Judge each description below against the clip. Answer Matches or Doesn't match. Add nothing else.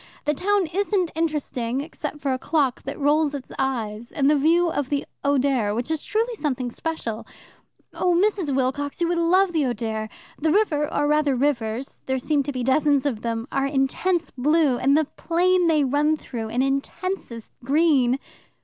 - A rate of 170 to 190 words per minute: Matches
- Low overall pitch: Doesn't match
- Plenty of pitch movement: Doesn't match